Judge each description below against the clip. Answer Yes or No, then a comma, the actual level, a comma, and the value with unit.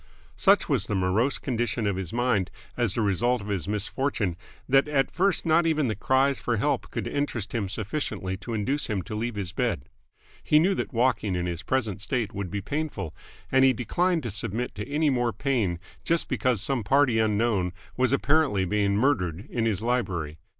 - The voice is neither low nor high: No, low, 115 Hz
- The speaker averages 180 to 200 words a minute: Yes, average, 190 wpm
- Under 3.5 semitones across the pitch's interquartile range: No, average, 5.1 semitones